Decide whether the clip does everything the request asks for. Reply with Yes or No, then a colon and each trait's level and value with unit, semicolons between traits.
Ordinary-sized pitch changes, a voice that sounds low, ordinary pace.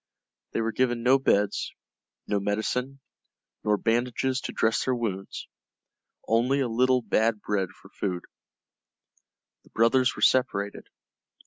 No: average, 3.6 semitones; low, 115 Hz; slow, 125 wpm